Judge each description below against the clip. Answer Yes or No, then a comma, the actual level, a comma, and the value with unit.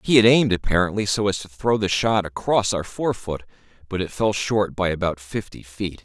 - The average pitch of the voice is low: Yes, low, 100 Hz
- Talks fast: Yes, fast, 220 wpm